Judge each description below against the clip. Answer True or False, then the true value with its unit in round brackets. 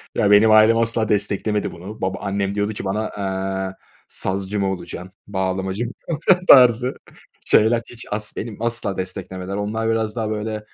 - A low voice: True (105 Hz)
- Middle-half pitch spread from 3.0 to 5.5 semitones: False (2.6 semitones)